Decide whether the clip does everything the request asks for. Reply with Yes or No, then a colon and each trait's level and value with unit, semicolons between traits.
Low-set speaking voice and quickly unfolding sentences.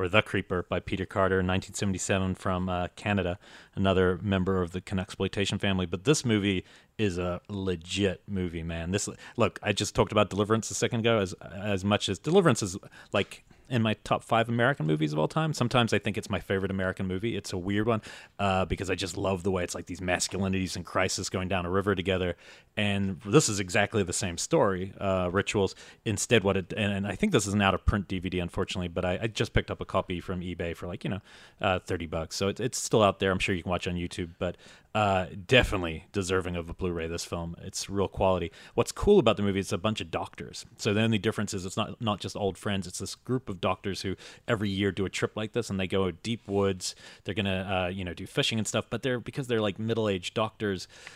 Yes: very low, 95 Hz; fast, 240 wpm